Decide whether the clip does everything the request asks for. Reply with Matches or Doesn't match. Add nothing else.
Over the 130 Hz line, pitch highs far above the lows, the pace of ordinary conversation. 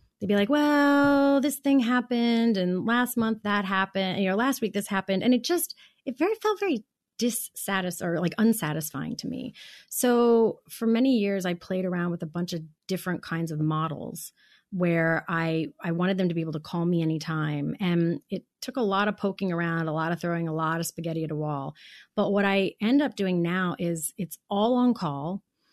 Doesn't match